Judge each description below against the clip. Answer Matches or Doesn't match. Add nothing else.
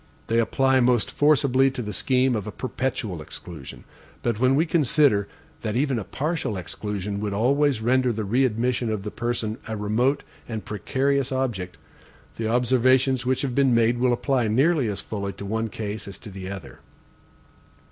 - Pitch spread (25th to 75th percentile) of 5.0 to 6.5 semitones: Doesn't match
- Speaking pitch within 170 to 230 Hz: Doesn't match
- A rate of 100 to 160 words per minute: Doesn't match